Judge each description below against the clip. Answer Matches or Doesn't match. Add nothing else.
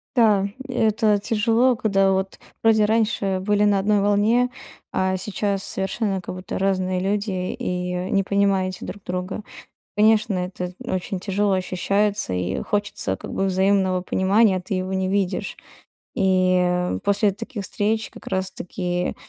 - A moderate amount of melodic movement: Doesn't match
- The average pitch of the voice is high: Matches